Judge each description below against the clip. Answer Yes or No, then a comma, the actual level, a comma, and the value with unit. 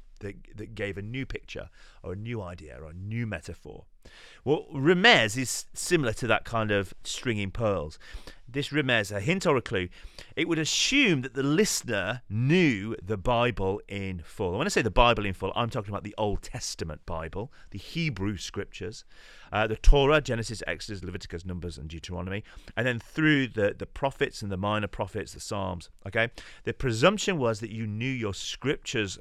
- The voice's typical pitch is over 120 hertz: No, low, 110 Hz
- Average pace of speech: Yes, average, 185 wpm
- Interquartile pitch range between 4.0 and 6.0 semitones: Yes, average, 4.7 semitones